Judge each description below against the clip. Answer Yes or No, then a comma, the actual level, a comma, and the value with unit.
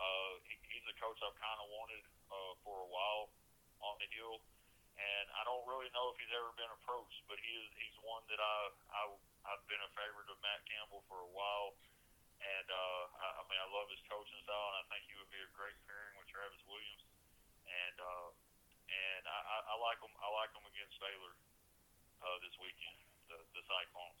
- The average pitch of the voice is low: Yes, low, 100 Hz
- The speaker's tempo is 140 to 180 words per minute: No, fast, 205 wpm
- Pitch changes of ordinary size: No, narrow, 2.0 semitones